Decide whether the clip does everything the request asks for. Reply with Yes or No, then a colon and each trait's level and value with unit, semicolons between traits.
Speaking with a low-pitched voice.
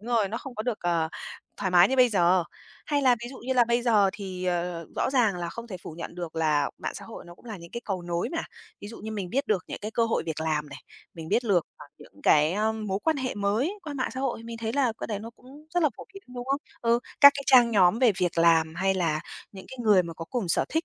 No: high, 210 Hz